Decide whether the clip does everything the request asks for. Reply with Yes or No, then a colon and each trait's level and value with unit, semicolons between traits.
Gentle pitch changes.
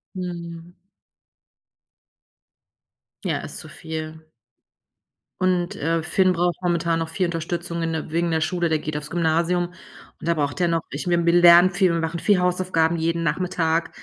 Yes: narrow, 1.5 semitones